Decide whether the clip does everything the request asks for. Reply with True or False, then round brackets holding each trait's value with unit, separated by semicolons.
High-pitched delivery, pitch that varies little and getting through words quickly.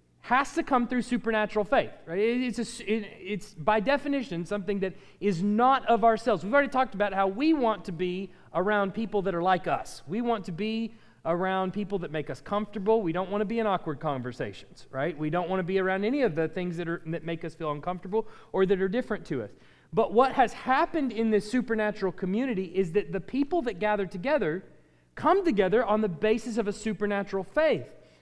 False (205 Hz; 3.7 semitones; 215 wpm)